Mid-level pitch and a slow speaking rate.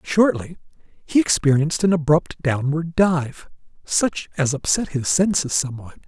Yes: medium, 155 Hz; slow, 130 wpm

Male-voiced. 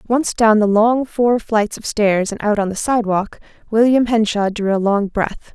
No: female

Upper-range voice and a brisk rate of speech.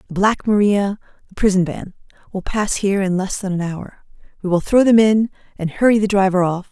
Yes: high, 195 Hz; fast, 215 wpm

